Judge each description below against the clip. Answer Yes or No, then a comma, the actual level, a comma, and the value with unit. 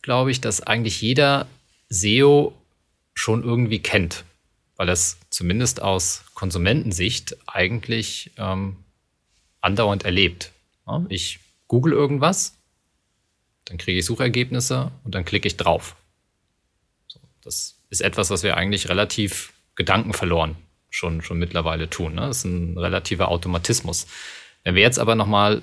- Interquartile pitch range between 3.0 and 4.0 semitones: No, average, 4.6 semitones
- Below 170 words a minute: Yes, slow, 125 wpm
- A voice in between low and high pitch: No, low, 100 Hz